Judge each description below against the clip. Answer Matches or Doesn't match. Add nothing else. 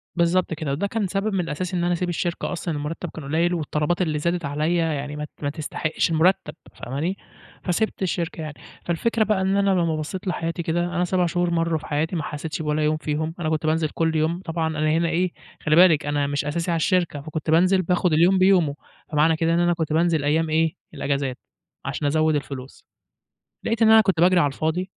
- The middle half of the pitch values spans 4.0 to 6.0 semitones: Doesn't match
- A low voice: Doesn't match